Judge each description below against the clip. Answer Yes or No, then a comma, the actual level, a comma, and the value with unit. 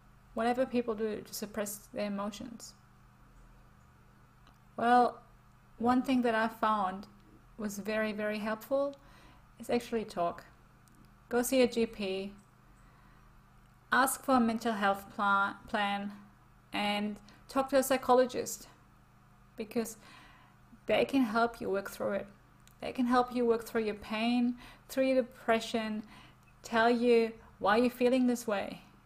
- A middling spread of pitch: Yes, average, 3.2 semitones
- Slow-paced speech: Yes, slow, 125 wpm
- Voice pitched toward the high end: Yes, high, 225 Hz